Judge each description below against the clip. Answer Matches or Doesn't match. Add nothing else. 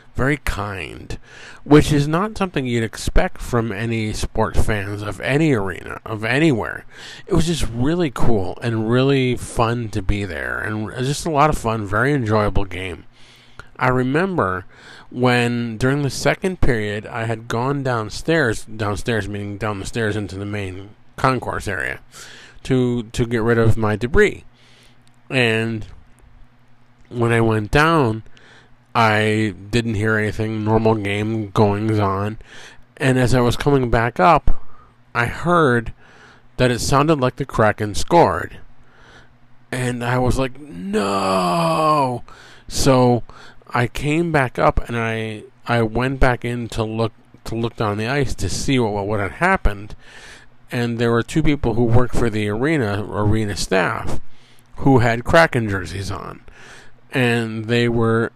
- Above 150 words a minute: Doesn't match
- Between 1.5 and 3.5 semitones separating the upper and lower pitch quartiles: Matches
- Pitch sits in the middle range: Doesn't match